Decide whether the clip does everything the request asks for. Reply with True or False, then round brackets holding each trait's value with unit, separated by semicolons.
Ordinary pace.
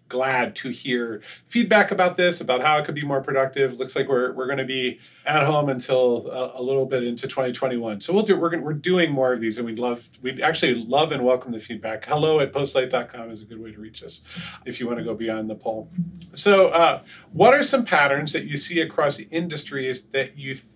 False (235 wpm)